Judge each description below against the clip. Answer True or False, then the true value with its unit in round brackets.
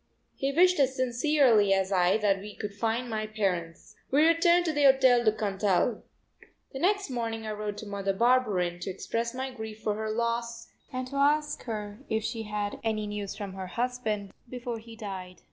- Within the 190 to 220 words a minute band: True (195 wpm)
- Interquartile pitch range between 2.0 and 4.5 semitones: True (3.8 semitones)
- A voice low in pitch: False (220 Hz)